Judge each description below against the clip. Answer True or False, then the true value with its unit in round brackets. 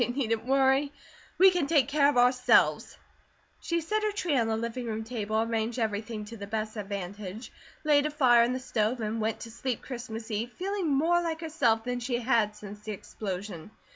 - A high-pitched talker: True (235 Hz)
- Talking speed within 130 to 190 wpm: False (200 wpm)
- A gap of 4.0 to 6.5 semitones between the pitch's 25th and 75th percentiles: True (4.3 semitones)